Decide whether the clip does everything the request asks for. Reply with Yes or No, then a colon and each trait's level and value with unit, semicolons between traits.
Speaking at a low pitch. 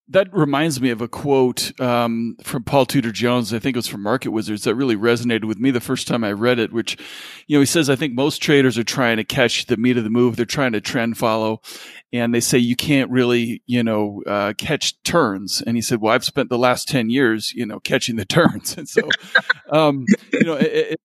Yes: low, 120 Hz